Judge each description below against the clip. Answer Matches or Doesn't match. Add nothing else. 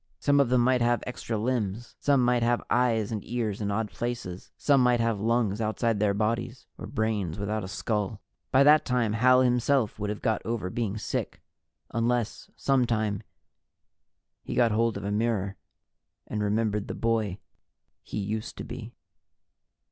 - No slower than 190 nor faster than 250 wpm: Doesn't match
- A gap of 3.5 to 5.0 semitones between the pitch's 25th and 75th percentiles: Doesn't match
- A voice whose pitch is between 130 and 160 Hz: Doesn't match